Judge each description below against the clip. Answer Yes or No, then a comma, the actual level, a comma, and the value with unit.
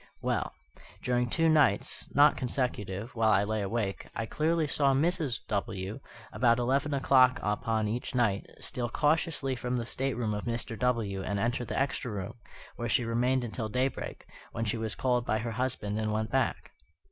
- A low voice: Yes, low, 120 Hz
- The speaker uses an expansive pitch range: No, average, 3.3 semitones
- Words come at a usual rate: Yes, average, 170 wpm